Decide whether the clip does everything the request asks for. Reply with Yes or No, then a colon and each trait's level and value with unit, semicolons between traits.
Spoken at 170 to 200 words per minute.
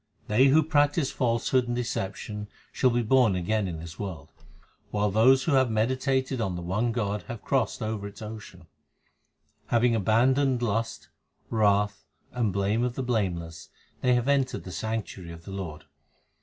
No: average, 160 wpm